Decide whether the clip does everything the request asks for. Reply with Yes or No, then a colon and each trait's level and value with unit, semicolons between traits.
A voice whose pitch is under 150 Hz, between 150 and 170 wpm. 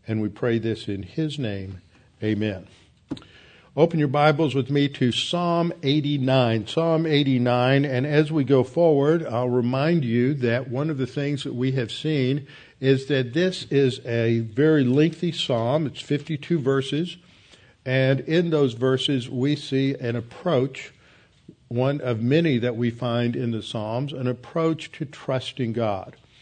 Yes: low, 135 Hz; average, 155 wpm